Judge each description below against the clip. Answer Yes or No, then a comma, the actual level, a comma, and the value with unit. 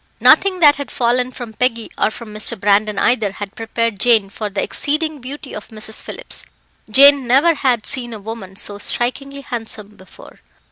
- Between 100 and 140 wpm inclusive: No, average, 175 wpm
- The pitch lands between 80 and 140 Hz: No, high, 235 Hz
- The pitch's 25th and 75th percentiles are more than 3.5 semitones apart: Yes, average, 4.3 semitones